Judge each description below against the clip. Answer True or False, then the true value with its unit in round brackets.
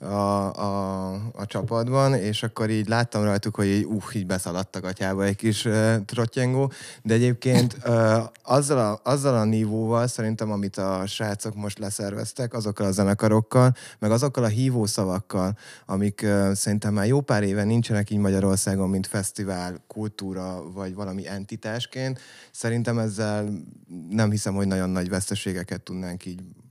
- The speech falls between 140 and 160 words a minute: True (150 wpm)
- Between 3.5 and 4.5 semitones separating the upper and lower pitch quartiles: False (2.8 semitones)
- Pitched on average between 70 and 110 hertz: True (105 Hz)